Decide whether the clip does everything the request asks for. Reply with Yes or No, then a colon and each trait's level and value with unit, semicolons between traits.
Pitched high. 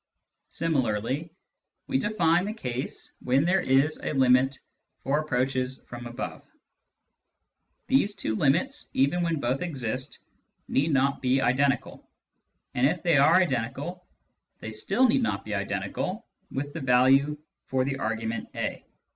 No: low, 135 Hz